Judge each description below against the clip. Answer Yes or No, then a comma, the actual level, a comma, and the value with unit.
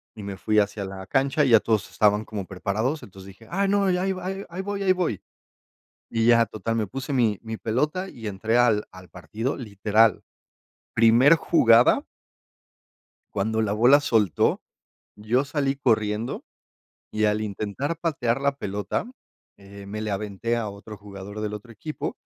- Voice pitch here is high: No, low, 110 Hz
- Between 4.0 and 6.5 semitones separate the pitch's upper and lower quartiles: Yes, average, 4.6 semitones